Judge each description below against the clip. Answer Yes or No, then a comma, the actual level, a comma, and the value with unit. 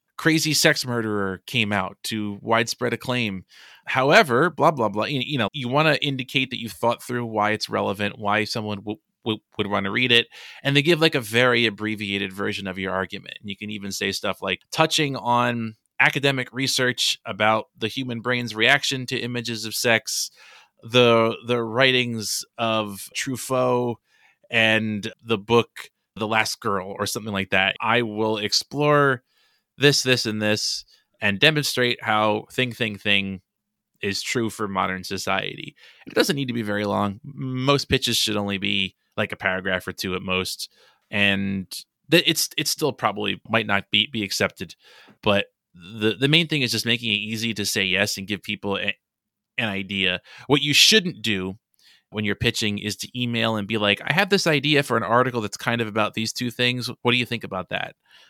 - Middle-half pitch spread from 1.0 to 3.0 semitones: No, average, 3.5 semitones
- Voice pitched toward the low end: Yes, low, 110 Hz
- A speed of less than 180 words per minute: No, average, 185 wpm